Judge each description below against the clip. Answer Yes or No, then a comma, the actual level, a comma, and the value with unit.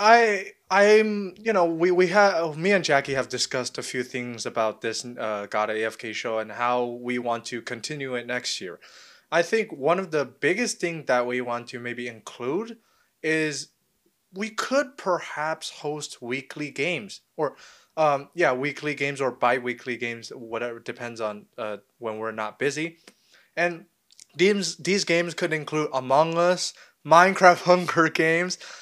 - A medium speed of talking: Yes, average, 165 wpm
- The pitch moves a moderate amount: No, wide, 6.6 semitones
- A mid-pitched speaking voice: Yes, medium, 150 Hz